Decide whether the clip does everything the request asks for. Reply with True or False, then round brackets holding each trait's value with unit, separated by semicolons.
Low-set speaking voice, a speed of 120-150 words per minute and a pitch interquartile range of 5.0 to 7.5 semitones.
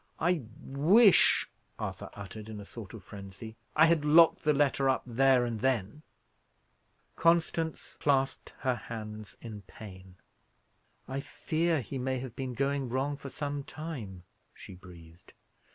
True (130 Hz; 140 wpm; 5.4 semitones)